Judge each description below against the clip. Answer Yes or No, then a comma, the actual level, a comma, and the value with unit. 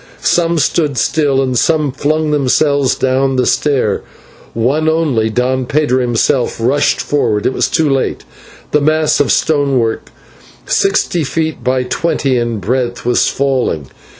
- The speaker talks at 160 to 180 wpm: No, average, 145 wpm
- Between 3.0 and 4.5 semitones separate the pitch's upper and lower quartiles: Yes, average, 3.4 semitones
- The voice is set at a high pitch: No, low, 135 Hz